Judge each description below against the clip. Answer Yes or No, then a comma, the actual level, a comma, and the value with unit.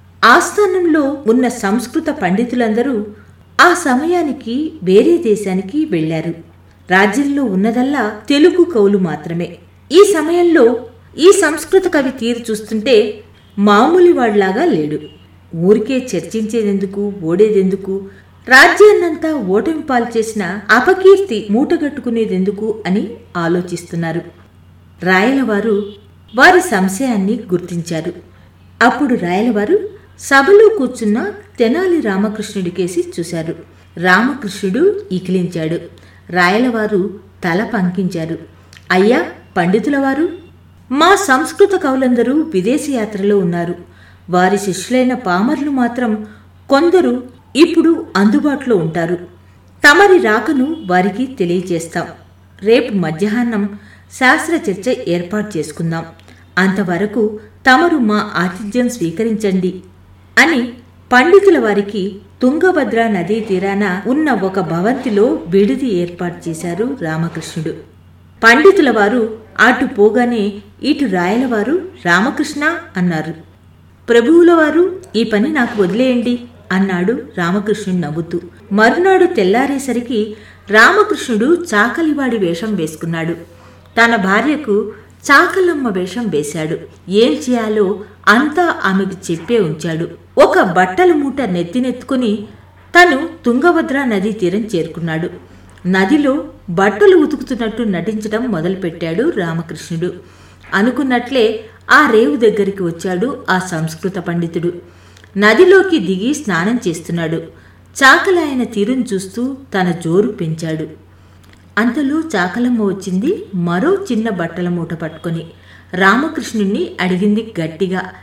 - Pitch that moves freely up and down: Yes, wide, 6.5 semitones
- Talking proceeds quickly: No, average, 90 wpm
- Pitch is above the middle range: Yes, high, 215 Hz